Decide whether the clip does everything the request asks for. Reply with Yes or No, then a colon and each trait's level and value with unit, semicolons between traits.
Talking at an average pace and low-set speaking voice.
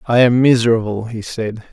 Yes: average, 175 wpm; low, 115 Hz